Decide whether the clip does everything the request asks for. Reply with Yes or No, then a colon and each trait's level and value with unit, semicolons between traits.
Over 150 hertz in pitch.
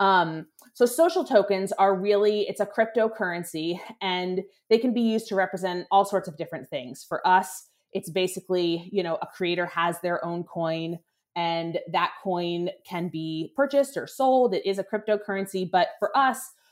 Yes: high, 190 Hz